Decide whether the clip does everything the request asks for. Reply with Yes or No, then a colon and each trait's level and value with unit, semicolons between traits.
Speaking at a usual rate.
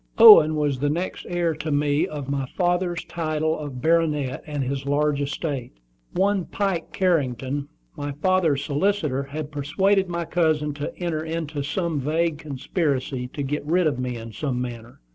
Yes: average, 160 wpm